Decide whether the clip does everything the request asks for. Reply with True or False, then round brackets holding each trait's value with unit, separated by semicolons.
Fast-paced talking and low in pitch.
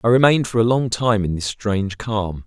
True (245 wpm; 110 Hz)